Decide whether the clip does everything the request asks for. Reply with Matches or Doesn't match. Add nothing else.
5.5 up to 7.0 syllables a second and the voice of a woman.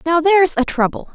Matches